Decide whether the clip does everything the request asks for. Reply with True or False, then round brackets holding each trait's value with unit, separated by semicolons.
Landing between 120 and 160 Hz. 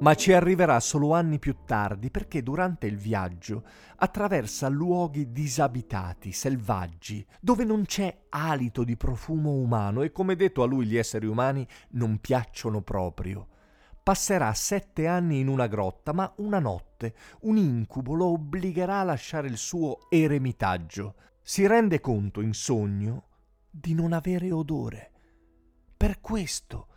True (135 Hz)